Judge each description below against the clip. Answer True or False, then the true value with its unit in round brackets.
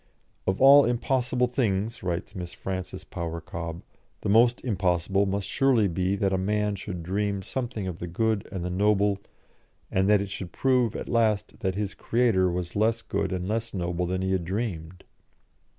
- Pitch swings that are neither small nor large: True (3.5 semitones)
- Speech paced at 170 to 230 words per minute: True (180 wpm)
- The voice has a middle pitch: False (100 Hz)